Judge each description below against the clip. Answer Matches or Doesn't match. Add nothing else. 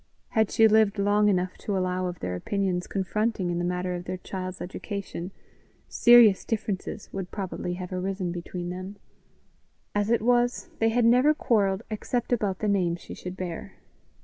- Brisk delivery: Doesn't match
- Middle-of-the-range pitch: Doesn't match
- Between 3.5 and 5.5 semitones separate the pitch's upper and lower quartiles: Doesn't match